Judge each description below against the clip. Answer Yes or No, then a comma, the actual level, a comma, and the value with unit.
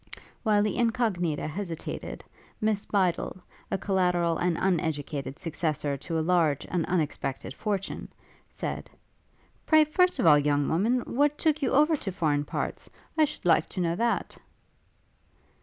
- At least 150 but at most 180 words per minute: No, average, 140 wpm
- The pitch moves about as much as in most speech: No, wide, 5.9 semitones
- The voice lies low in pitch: No, medium, 180 Hz